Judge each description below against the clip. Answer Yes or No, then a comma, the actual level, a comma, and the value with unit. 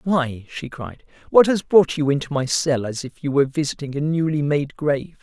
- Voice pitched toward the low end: No, medium, 145 Hz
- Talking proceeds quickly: Yes, fast, 220 wpm